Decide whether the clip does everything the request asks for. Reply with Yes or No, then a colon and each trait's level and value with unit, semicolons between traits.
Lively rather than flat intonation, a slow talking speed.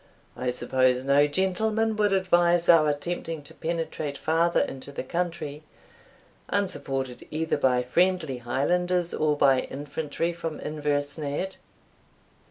No: average, 3.7 semitones; slow, 115 wpm